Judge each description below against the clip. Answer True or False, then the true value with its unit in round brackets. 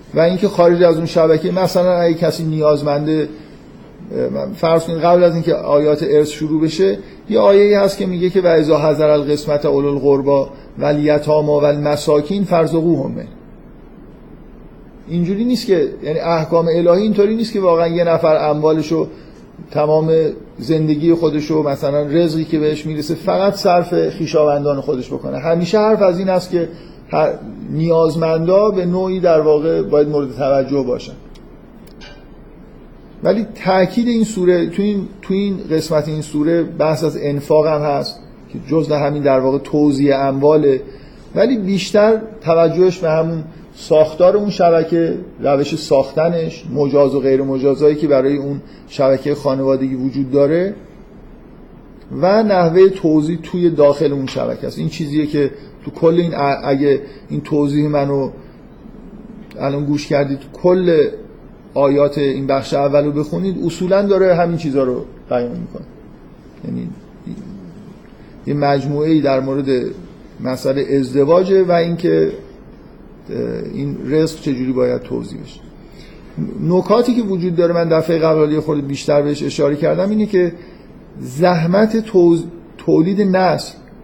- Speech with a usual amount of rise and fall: True (3.6 semitones)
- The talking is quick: False (140 wpm)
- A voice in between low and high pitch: True (160 Hz)